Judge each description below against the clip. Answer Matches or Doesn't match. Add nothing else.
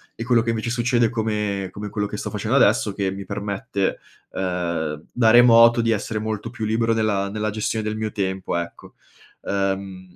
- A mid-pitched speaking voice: Doesn't match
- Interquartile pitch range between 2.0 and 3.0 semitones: Matches